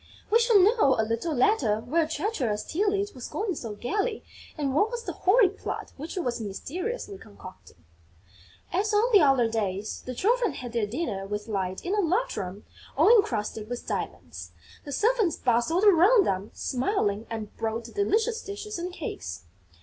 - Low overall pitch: No, very high, 310 Hz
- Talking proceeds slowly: No, average, 170 wpm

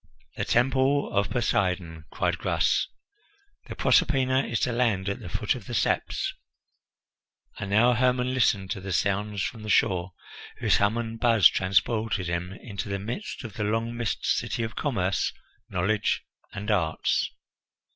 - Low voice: Yes, low, 105 Hz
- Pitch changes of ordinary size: Yes, average, 3.6 semitones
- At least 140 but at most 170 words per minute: Yes, average, 155 wpm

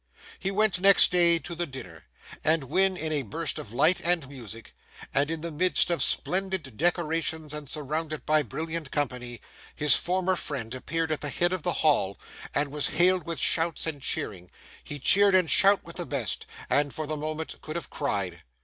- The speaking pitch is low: No, medium, 155 Hz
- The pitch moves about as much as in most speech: Yes, average, 3.5 semitones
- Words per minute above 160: Yes, average, 190 wpm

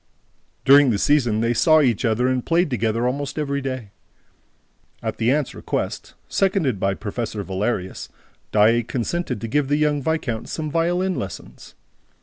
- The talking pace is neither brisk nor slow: Yes, average, 150 wpm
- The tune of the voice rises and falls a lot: No, average, 4.8 semitones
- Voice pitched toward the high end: No, low, 130 Hz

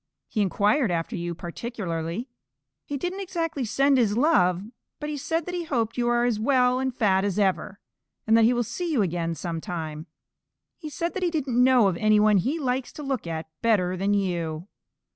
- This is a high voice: Yes, high, 225 Hz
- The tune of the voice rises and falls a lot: Yes, wide, 6.9 semitones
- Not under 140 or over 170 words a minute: No, average, 200 wpm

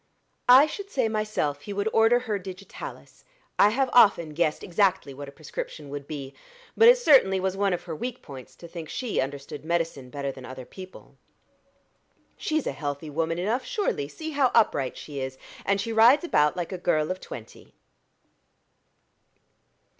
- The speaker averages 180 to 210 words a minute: No, average, 170 wpm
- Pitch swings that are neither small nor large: No, wide, 7.6 semitones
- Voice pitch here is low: No, medium, 180 Hz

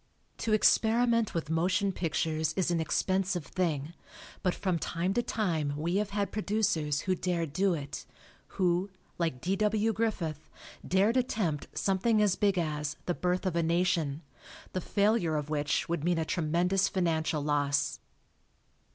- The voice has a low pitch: No, medium, 175 Hz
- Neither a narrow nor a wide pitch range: Yes, average, 4.0 semitones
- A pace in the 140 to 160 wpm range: Yes, average, 150 wpm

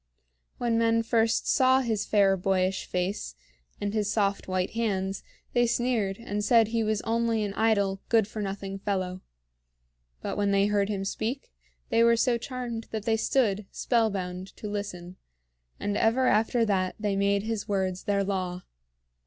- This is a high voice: Yes, high, 205 Hz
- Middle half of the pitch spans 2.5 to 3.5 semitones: Yes, average, 2.8 semitones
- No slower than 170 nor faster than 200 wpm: No, average, 160 wpm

